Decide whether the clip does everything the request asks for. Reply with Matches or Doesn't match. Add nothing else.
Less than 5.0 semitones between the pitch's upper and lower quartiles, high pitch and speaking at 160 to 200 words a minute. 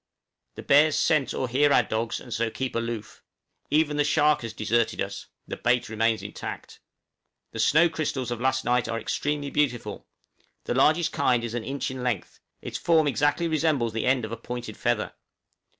Doesn't match